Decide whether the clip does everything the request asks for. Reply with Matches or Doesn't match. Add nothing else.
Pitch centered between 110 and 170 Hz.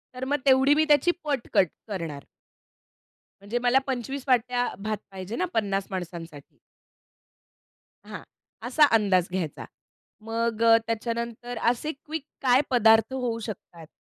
Doesn't match